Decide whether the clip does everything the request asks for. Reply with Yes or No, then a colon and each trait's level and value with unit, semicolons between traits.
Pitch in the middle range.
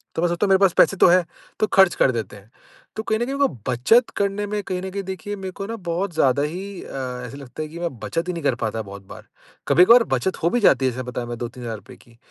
Yes: medium, 170 Hz